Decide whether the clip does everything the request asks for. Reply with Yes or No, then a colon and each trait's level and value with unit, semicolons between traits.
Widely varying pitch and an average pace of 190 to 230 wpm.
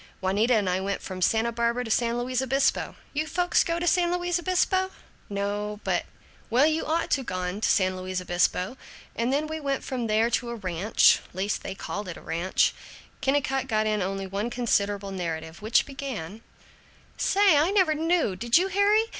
Yes: wide, 7.4 semitones; average, 195 wpm